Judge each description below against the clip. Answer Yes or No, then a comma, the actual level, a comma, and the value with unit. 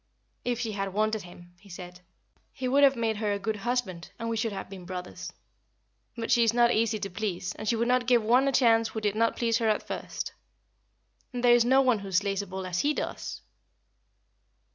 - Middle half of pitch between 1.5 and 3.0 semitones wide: No, average, 3.4 semitones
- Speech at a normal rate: No, fast, 225 wpm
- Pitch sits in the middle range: No, high, 220 Hz